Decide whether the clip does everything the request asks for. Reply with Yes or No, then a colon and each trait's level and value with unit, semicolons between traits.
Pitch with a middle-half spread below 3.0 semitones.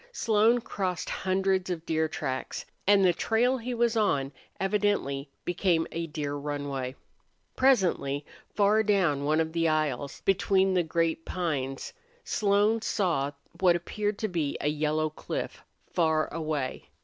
No: average, 5.2 semitones